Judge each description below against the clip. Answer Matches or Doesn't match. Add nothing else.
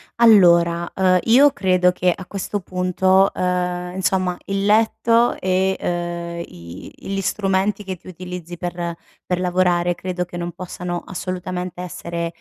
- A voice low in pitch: Doesn't match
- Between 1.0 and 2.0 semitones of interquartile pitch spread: Matches